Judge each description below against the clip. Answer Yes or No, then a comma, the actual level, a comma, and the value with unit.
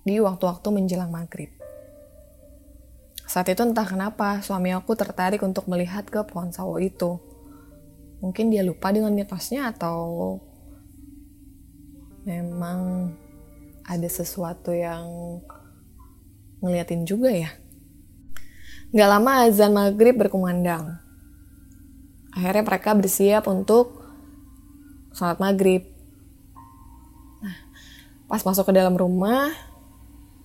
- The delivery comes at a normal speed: Yes, average, 95 wpm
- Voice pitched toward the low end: No, medium, 180 Hz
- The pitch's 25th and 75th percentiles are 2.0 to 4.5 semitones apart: No, wide, 5.6 semitones